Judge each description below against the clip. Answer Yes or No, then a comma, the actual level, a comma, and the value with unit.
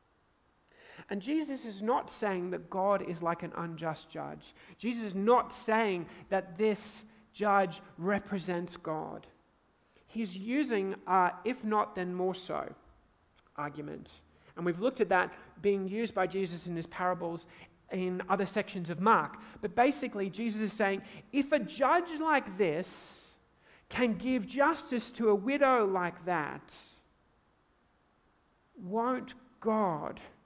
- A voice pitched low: No, high, 195 Hz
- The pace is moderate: No, slow, 130 wpm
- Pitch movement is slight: No, average, 4.4 semitones